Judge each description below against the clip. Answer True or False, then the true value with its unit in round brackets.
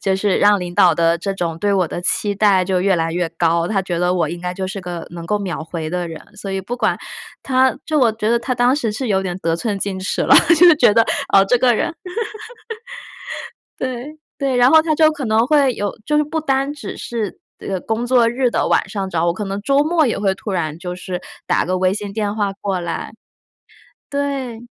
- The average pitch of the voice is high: True (205 Hz)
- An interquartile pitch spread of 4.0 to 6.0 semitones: True (5.6 semitones)